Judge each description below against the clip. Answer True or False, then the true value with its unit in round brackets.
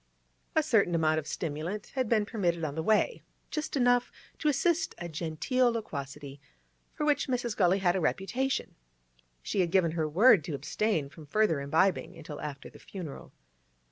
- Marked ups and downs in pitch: True (7.1 semitones)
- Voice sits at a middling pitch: True (180 Hz)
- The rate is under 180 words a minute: True (170 wpm)